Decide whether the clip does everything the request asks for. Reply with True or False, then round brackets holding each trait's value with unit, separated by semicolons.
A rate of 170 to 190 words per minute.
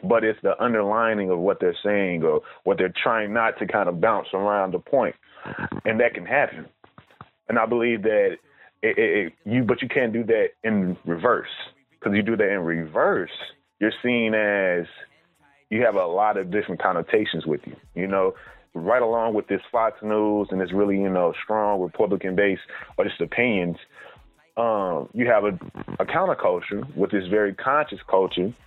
True (180 wpm)